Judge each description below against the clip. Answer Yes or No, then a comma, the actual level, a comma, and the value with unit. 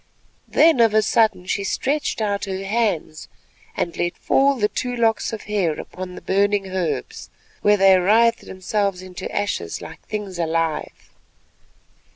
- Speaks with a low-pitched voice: No, high, 200 Hz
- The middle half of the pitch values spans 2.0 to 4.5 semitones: Yes, average, 3.4 semitones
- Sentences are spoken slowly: No, average, 150 wpm